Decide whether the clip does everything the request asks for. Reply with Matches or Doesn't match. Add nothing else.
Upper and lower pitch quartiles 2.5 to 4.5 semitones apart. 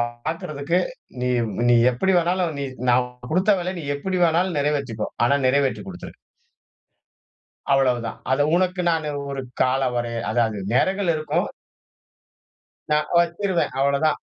Doesn't match